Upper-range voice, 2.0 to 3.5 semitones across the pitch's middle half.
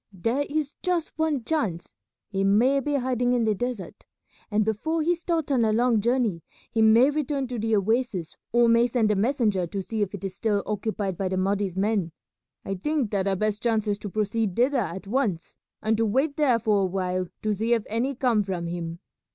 No: high, 220 Hz; average, 4.2 semitones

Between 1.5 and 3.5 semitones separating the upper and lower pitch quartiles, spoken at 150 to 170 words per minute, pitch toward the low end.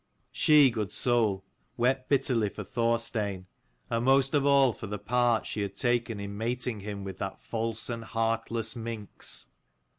Yes: average, 2.8 semitones; average, 155 wpm; low, 115 Hz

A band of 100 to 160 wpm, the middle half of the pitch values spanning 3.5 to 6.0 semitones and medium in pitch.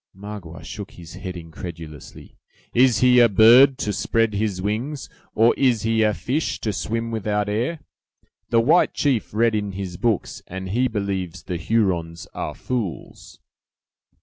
No: average, 150 wpm; average, 3.9 semitones; low, 105 Hz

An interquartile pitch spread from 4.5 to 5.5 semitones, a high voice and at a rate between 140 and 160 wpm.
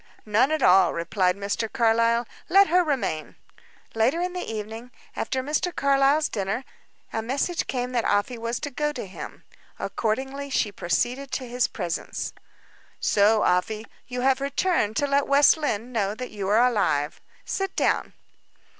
Yes: average, 4.8 semitones; high, 245 Hz; average, 155 wpm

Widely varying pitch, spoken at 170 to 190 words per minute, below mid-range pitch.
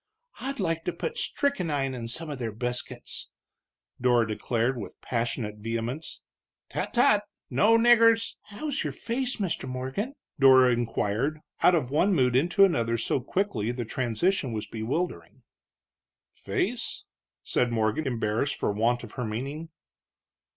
No: wide, 7.6 semitones; average, 140 wpm; low, 130 Hz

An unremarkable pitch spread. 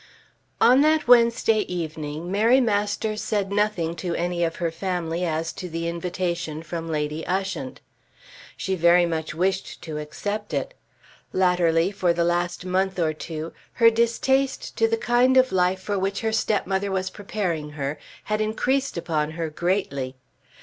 Yes: average, 4.3 semitones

